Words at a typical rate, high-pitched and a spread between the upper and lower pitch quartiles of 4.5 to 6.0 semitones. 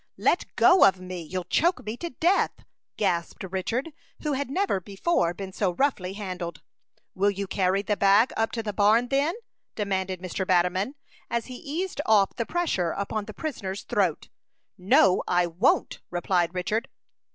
Yes: average, 165 wpm; high, 200 Hz; average, 5.1 semitones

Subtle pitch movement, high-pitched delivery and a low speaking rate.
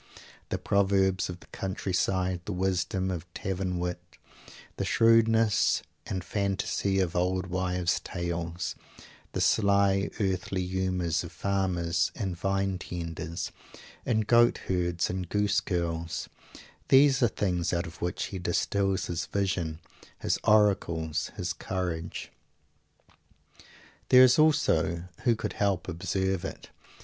No: narrow, 2.2 semitones; very low, 95 Hz; slow, 125 wpm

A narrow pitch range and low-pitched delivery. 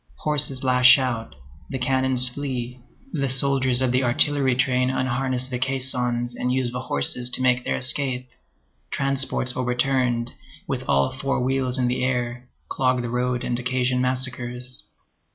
Yes: narrow, 1.1 semitones; low, 125 Hz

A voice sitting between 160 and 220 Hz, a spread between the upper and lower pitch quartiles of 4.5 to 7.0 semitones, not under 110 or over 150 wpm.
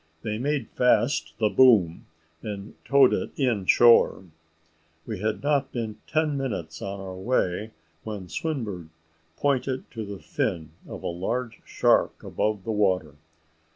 No: low, 110 Hz; average, 5.0 semitones; average, 140 wpm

